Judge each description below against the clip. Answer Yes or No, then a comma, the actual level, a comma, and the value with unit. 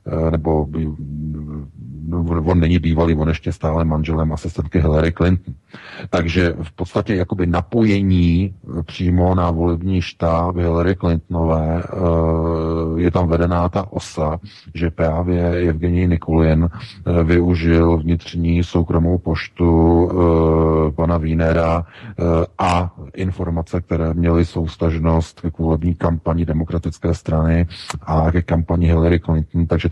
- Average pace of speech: No, slow, 105 wpm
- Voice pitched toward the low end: Yes, very low, 85 Hz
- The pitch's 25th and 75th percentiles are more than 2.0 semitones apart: No, narrow, 1.4 semitones